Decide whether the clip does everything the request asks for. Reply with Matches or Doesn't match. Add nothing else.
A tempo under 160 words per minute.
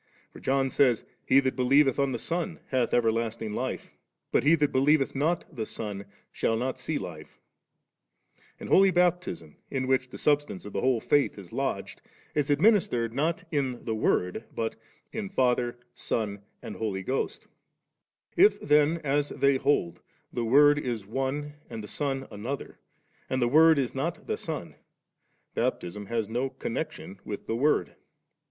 Doesn't match